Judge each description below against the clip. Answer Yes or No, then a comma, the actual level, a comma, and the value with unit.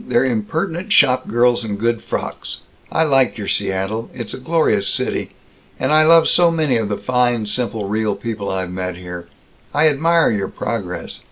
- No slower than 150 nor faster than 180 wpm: Yes, average, 170 wpm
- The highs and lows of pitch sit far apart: Yes, wide, 6.0 semitones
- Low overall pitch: Yes, low, 115 Hz